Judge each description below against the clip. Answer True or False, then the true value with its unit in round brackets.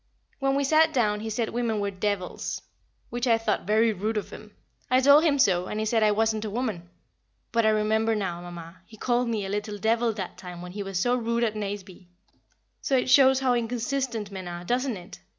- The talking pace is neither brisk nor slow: False (220 wpm)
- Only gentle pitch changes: False (3.3 semitones)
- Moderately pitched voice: False (220 Hz)